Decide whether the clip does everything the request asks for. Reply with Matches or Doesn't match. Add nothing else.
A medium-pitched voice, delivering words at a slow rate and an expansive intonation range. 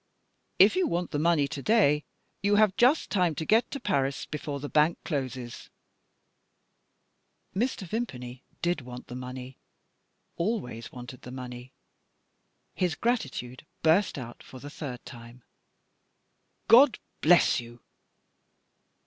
Matches